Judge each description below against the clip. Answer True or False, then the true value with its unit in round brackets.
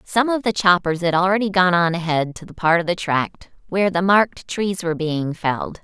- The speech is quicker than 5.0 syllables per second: True (5.4 syllables/s)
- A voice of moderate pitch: True (180 Hz)